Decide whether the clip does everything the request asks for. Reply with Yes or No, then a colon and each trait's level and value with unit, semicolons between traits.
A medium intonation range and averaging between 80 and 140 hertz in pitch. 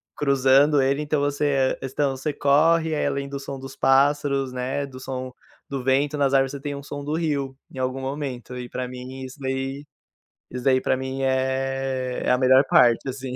No: narrow, 1.4 semitones; low, 135 Hz